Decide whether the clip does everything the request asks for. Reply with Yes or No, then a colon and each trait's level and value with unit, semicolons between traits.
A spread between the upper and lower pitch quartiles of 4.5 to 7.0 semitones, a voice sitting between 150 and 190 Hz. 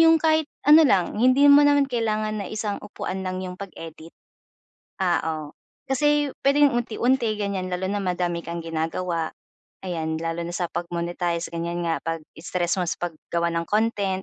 Yes: average, 5.0 semitones; medium, 185 Hz